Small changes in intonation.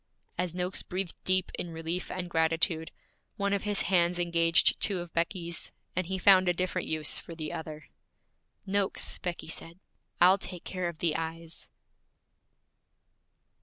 Yes: narrow, 2.0 semitones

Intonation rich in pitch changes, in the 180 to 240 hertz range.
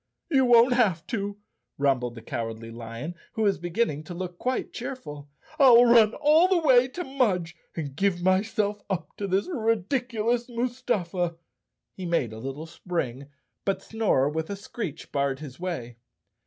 Yes: wide, 8.1 semitones; high, 190 Hz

